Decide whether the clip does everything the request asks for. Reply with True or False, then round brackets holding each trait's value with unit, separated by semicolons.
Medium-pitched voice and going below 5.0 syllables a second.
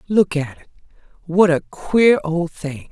True (170 Hz; 3.9 syllables/s)